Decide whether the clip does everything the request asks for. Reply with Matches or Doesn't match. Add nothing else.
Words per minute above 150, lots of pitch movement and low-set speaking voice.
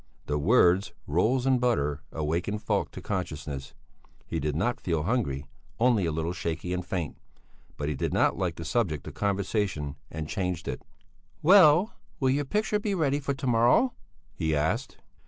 Matches